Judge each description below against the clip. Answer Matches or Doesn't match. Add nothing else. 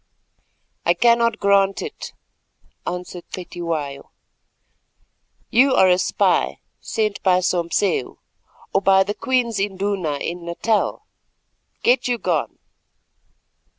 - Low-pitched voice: Doesn't match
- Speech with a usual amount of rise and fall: Matches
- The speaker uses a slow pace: Matches